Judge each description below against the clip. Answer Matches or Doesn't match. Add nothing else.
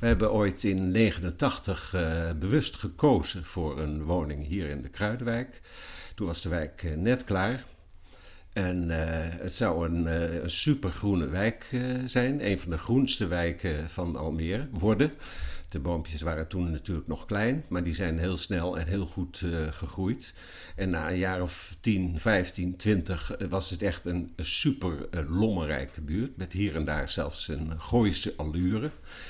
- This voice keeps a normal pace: Matches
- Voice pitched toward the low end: Matches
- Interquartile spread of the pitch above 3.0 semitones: Matches